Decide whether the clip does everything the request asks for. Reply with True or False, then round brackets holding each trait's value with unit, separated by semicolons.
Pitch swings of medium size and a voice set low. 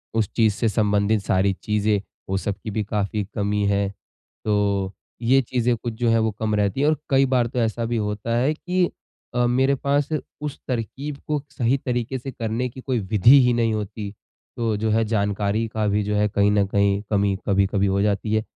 True (3.1 semitones; 110 Hz)